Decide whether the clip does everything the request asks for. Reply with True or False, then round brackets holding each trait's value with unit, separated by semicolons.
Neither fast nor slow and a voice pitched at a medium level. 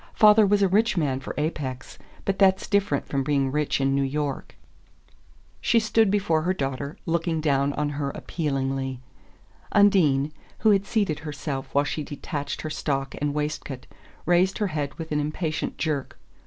True (165 wpm; 150 Hz)